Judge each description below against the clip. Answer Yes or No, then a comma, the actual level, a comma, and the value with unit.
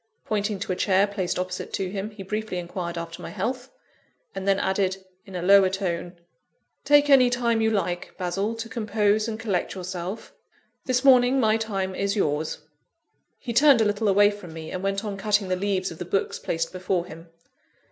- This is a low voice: No, high, 195 Hz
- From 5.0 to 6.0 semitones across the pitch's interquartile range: No, average, 3.0 semitones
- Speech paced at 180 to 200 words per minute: Yes, average, 190 wpm